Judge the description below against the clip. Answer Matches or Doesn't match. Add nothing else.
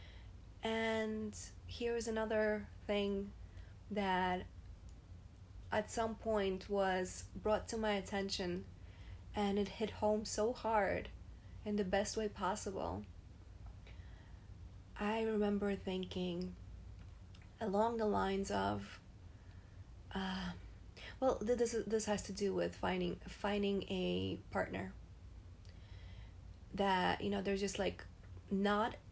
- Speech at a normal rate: Doesn't match